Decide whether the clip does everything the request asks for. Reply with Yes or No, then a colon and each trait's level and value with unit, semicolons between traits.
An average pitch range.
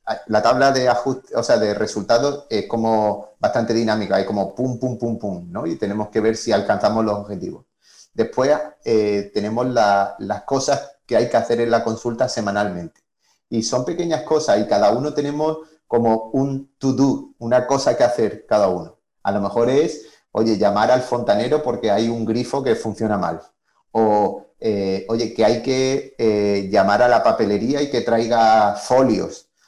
Yes: average, 3.9 semitones